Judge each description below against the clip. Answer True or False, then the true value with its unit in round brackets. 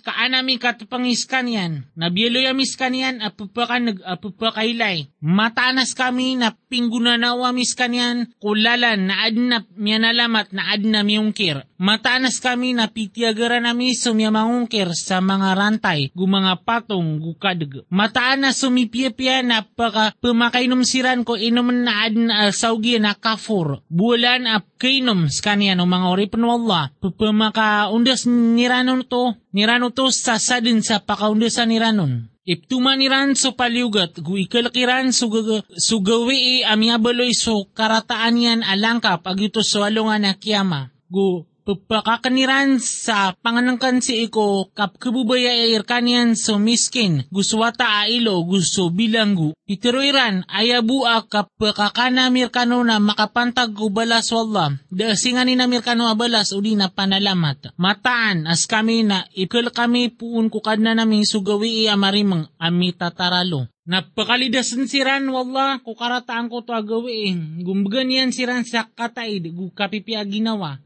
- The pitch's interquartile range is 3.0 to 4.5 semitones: True (3.3 semitones)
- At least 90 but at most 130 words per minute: True (125 wpm)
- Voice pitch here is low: False (225 Hz)